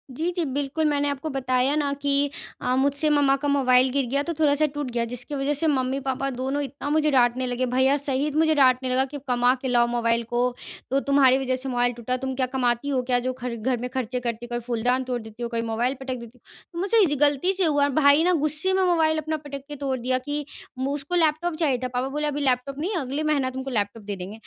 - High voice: Yes, very high, 265 Hz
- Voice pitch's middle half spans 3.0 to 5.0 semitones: No, narrow, 2.6 semitones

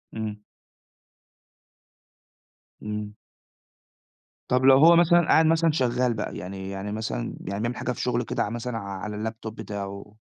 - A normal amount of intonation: Yes, average, 3.6 semitones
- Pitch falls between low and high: No, low, 110 Hz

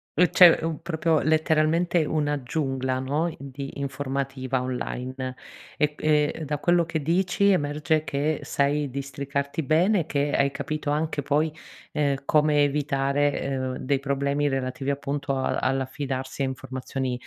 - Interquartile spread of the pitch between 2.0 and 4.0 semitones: Yes, narrow, 2.4 semitones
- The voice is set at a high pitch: No, medium, 145 Hz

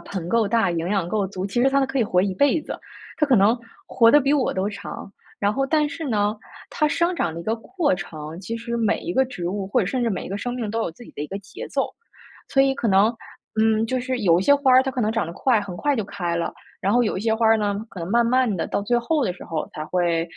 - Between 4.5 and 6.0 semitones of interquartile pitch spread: Yes, average, 5.1 semitones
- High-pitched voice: Yes, high, 220 Hz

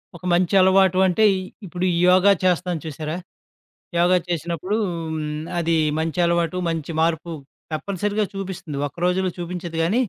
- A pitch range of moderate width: No, narrow, 2.1 semitones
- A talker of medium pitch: Yes, medium, 175 Hz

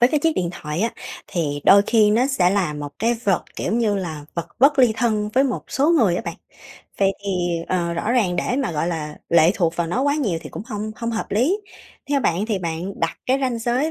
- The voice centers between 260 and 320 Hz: No, high, 210 Hz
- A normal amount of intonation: No, wide, 6.3 semitones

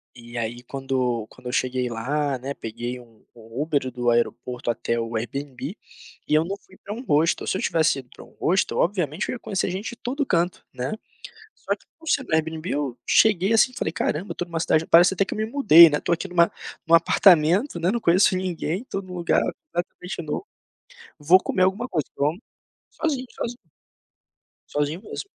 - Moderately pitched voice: Yes, medium, 165 Hz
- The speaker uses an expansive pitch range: Yes, wide, 6.7 semitones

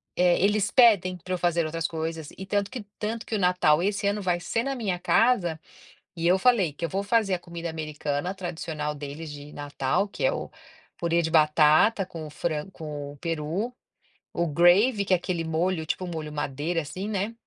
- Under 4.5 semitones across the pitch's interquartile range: Yes, average, 4.0 semitones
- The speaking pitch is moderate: Yes, medium, 175 Hz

